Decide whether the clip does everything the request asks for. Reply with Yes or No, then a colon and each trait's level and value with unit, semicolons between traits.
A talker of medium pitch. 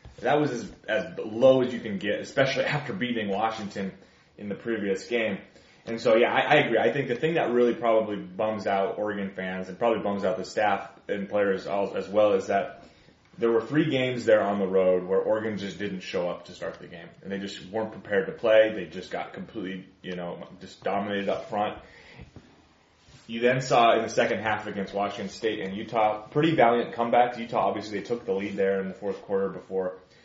No: low, 105 Hz